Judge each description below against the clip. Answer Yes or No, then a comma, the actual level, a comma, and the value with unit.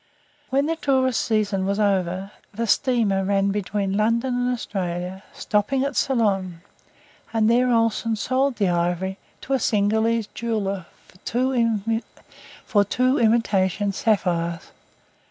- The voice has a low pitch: No, high, 210 Hz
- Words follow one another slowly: Yes, slow, 120 wpm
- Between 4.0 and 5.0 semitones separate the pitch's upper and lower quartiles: No, average, 3.5 semitones